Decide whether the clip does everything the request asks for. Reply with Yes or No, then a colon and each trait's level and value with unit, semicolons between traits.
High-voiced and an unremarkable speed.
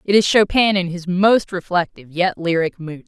No: medium, 180 Hz; average, 195 wpm